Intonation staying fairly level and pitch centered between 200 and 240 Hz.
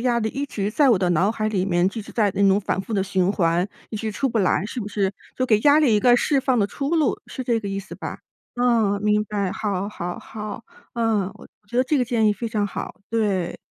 No: average, 3.3 semitones; high, 210 Hz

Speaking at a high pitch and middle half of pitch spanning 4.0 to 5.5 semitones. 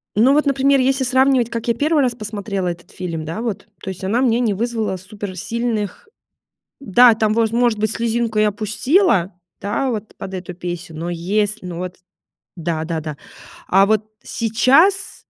Yes: high, 215 Hz; average, 4.6 semitones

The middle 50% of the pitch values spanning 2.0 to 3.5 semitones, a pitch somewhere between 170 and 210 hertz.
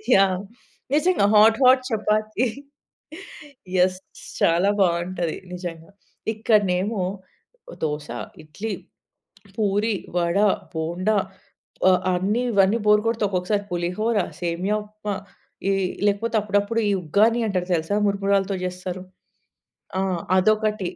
Yes: average, 3.0 semitones; high, 200 Hz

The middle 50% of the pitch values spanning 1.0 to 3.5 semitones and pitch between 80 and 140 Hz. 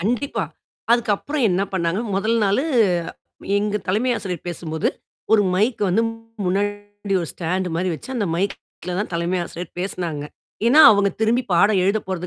No: average, 3.2 semitones; high, 195 Hz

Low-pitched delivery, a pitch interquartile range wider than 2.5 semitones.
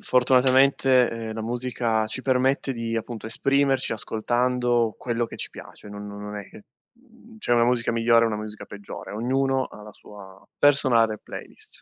Yes: low, 120 Hz; average, 2.9 semitones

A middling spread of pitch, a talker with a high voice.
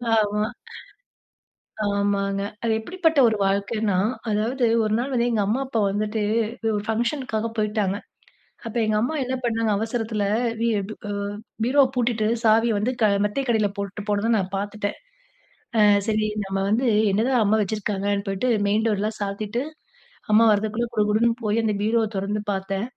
No: narrow, 2.2 semitones; high, 215 Hz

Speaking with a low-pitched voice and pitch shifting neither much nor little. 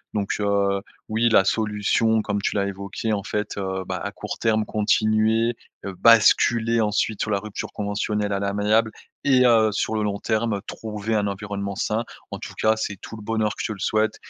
No: low, 105 Hz; narrow, 1.6 semitones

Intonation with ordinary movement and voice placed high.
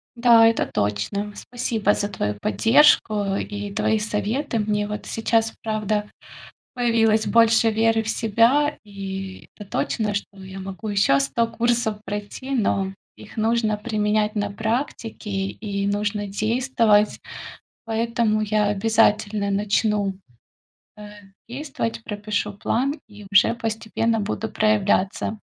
No: narrow, 1.8 semitones; high, 215 Hz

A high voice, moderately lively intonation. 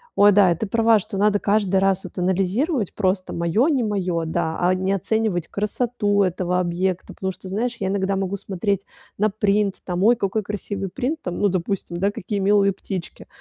No: high, 195 Hz; narrow, 2.2 semitones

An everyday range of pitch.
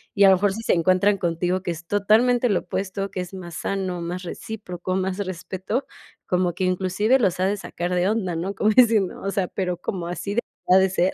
No: narrow, 2.0 semitones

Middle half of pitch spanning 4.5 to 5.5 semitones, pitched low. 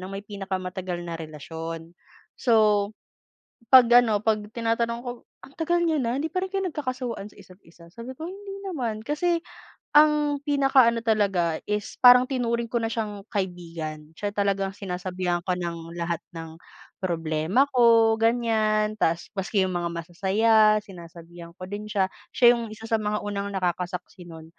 No: average, 5.1 semitones; high, 210 Hz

